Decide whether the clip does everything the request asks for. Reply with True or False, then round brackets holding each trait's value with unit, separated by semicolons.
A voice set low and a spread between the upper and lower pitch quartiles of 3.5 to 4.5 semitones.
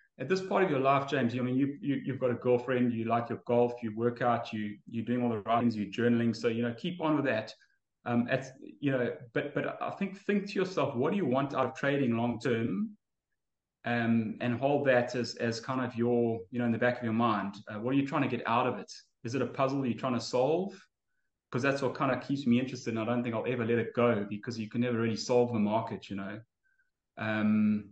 False (120 Hz; 2.4 semitones)